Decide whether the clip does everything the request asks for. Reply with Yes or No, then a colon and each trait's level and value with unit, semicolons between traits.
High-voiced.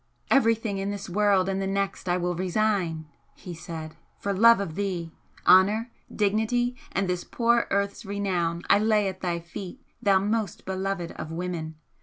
Yes: high, 195 Hz